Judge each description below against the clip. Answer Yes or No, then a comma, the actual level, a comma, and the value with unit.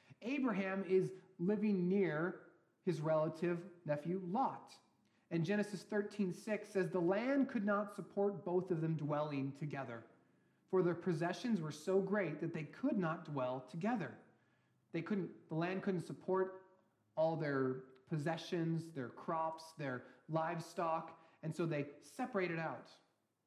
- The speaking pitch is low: No, medium, 175 Hz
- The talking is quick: No, slow, 135 wpm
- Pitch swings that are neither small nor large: Yes, average, 3.3 semitones